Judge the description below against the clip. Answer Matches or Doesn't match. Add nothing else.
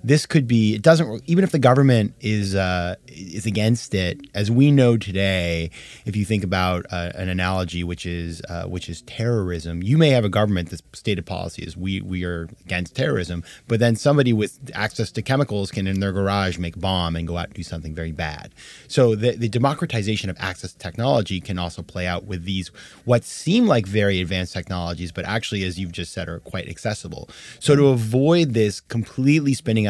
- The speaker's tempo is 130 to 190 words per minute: Doesn't match